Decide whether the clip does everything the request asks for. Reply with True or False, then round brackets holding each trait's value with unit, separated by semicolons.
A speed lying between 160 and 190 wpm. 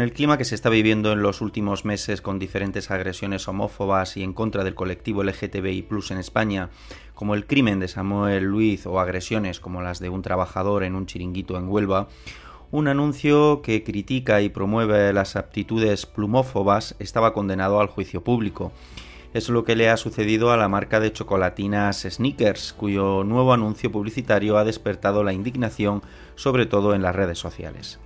True (175 wpm)